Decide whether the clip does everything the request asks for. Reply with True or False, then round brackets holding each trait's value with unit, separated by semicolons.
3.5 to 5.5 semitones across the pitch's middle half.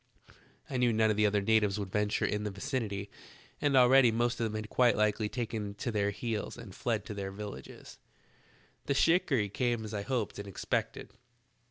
False (2.8 semitones)